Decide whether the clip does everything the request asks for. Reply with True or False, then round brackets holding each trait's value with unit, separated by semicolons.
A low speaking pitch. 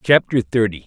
True (115 Hz)